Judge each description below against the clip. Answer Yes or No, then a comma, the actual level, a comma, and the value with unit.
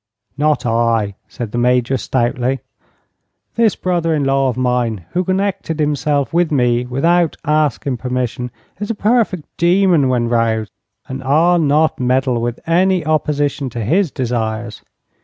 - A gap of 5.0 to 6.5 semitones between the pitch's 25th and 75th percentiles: Yes, average, 5.3 semitones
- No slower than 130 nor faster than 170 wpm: Yes, average, 140 wpm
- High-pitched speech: No, low, 135 Hz